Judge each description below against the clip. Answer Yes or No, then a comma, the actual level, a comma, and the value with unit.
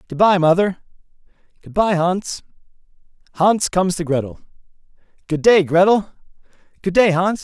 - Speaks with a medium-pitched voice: Yes, medium, 180 Hz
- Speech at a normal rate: No, slow, 115 wpm